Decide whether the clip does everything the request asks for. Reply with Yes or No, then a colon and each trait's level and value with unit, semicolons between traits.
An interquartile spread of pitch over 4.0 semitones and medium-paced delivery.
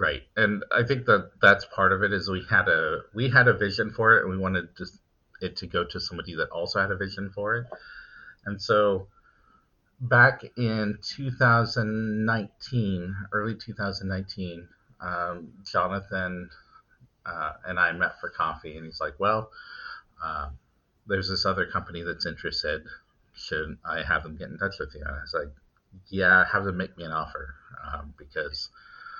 No: average, 3.3 semitones; average, 175 wpm